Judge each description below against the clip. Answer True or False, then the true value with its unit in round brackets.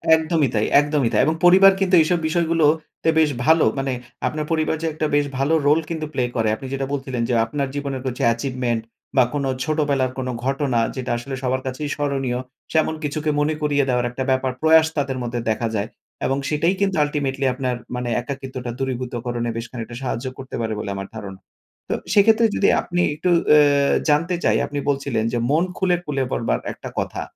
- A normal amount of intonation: True (3.6 semitones)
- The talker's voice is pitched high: False (140 Hz)